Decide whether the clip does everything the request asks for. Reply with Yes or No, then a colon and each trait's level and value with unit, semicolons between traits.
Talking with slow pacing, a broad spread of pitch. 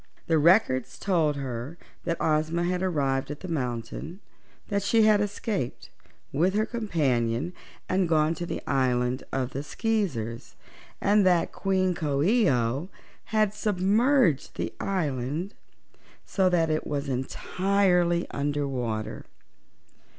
Yes: slow, 130 wpm; wide, 6.3 semitones